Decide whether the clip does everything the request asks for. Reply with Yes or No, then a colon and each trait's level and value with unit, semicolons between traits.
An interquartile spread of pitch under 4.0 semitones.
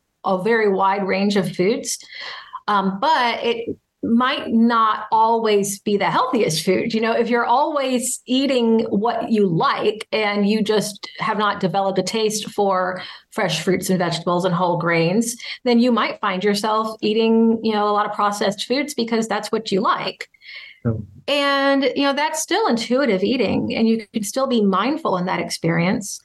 Yes: average, 3.5 semitones